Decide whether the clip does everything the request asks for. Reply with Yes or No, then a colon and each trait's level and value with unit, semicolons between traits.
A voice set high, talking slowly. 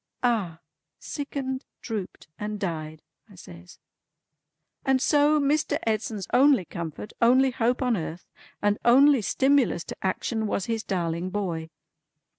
Yes: high, 220 Hz; slow, 125 wpm